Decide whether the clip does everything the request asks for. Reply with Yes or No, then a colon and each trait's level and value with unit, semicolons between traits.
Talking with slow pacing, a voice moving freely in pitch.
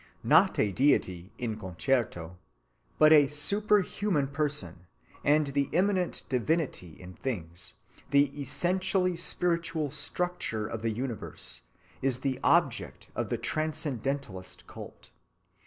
Yes: slow, 110 wpm; wide, 6.8 semitones